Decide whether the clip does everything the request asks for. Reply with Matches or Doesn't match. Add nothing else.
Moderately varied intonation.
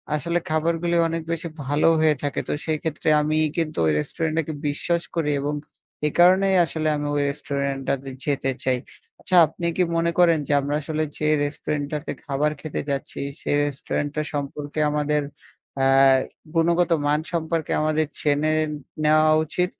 Doesn't match